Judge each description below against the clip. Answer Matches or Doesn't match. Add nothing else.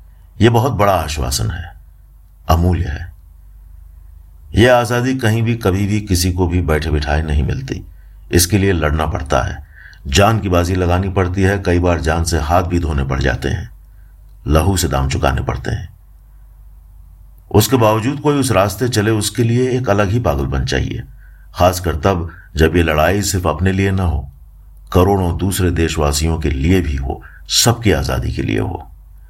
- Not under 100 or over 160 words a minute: Doesn't match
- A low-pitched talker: Matches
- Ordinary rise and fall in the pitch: Matches